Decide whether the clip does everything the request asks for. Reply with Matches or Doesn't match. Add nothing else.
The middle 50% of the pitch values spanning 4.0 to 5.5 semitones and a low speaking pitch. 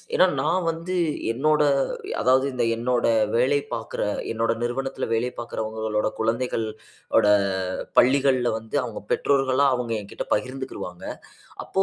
Doesn't match